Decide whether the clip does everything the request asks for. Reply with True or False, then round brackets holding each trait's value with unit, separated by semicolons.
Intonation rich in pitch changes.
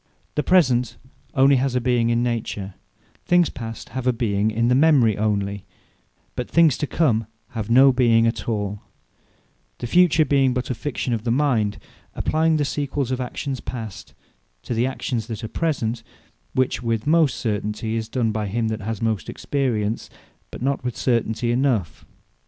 False (3.4 semitones)